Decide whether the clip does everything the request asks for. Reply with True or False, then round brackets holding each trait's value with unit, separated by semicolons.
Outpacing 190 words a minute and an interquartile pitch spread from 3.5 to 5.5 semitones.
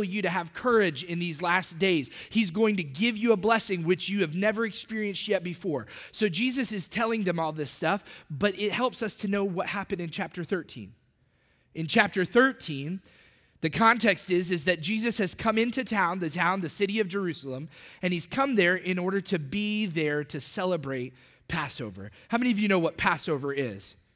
True (200 wpm; 4.5 semitones)